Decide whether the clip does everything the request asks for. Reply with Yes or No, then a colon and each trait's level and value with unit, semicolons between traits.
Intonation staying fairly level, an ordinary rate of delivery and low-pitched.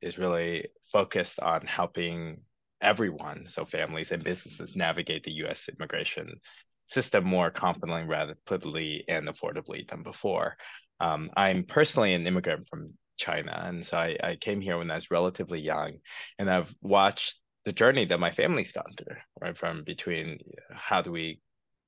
Yes: narrow, 1.7 semitones; average, 155 wpm; very low, 85 Hz